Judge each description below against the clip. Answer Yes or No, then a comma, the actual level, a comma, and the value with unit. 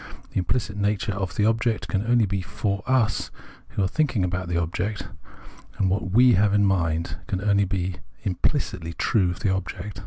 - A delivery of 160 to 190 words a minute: Yes, average, 185 wpm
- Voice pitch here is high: No, low, 100 Hz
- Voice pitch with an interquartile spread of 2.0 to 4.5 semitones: Yes, average, 2.7 semitones